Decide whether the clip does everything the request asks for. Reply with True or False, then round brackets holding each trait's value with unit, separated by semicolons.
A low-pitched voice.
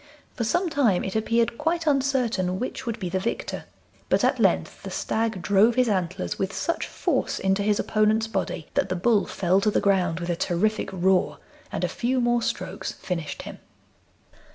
False (210 Hz)